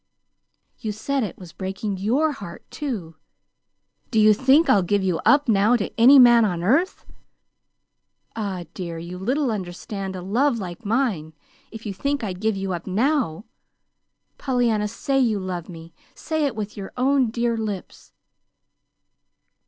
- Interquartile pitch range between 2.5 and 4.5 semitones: No, average, 5.0 semitones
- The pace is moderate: Yes, average, 150 wpm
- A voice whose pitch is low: No, high, 215 Hz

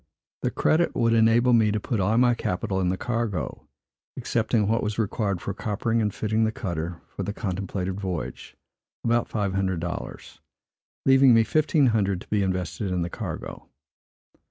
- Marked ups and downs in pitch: No, average, 3.6 semitones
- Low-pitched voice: Yes, low, 105 Hz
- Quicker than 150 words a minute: Yes, average, 170 wpm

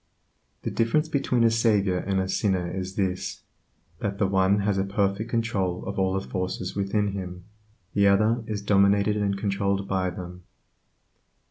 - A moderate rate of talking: Yes, average, 160 wpm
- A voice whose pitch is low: Yes, low, 100 Hz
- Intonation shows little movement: Yes, narrow, 1.7 semitones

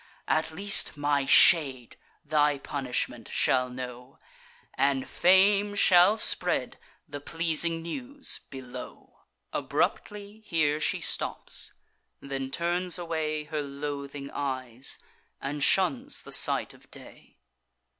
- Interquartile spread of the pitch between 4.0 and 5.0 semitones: Yes, average, 4.4 semitones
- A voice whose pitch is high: No, medium, 150 Hz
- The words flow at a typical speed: No, slow, 105 wpm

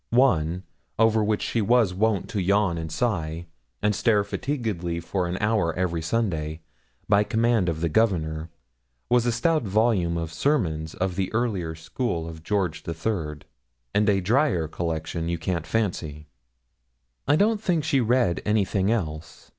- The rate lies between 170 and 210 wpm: No, average, 155 wpm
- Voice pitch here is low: Yes, very low, 95 Hz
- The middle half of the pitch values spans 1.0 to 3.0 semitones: No, average, 5.3 semitones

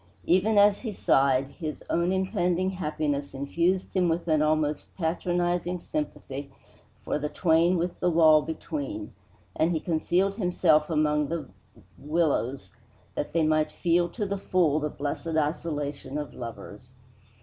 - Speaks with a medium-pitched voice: Yes, medium, 165 Hz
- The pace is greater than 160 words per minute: No, average, 140 wpm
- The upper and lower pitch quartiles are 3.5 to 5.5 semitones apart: No, average, 3.1 semitones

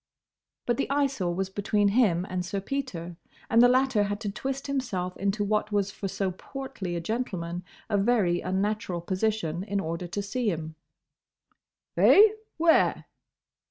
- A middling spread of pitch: Yes, average, 4.9 semitones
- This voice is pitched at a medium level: No, high, 200 Hz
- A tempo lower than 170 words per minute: Yes, average, 155 wpm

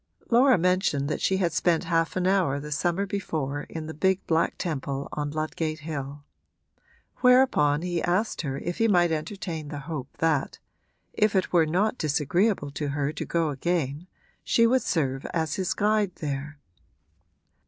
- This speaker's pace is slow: No, average, 165 wpm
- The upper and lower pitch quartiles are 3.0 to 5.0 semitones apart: Yes, average, 4.2 semitones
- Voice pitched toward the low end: No, medium, 165 Hz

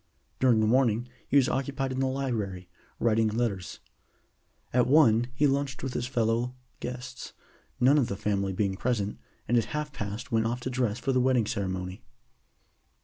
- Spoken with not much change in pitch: No, average, 3.6 semitones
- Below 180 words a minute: Yes, average, 170 wpm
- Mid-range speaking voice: No, low, 120 Hz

